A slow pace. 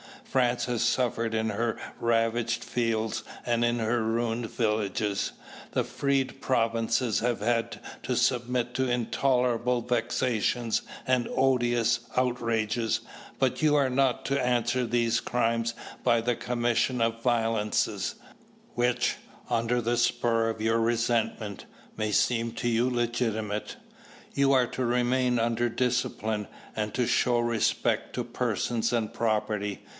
Yes: slow, 130 wpm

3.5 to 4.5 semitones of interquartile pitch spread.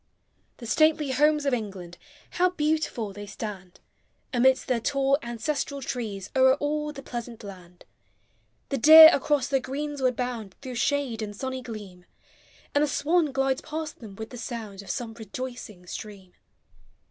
No: average, 5.0 semitones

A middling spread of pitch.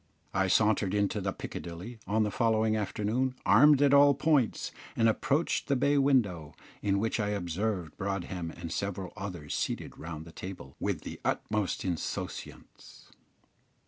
Yes: average, 4.2 semitones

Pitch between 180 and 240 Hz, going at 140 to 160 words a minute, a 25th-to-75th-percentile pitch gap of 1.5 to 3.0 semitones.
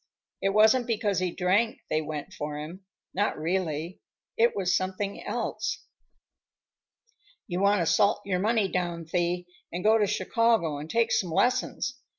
No: medium, 185 Hz; average, 155 wpm; average, 3.9 semitones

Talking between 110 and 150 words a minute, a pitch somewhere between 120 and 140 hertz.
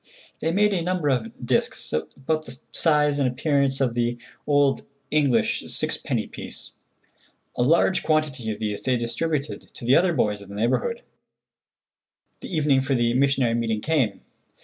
No: average, 160 wpm; low, 135 Hz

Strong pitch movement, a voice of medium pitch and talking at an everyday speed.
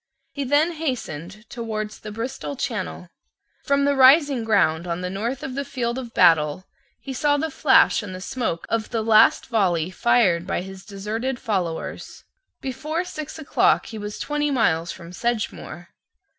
No: wide, 6.5 semitones; high, 225 Hz; average, 160 wpm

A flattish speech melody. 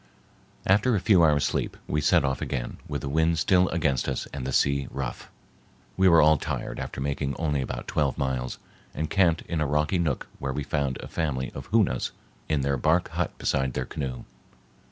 No: average, 3.3 semitones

